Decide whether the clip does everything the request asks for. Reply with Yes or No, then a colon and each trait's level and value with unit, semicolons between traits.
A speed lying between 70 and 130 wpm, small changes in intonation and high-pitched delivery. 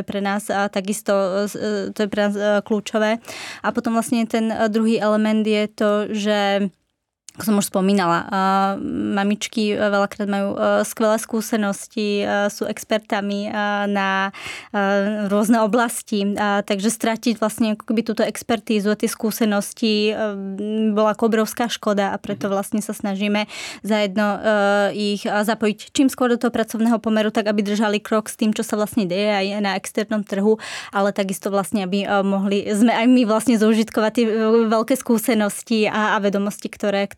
No: average, 145 wpm; narrow, 1.7 semitones; high, 210 Hz